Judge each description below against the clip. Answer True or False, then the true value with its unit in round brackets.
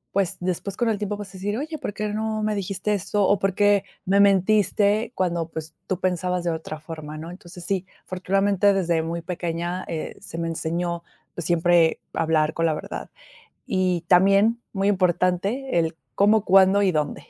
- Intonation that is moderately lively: True (3.0 semitones)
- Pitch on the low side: False (185 Hz)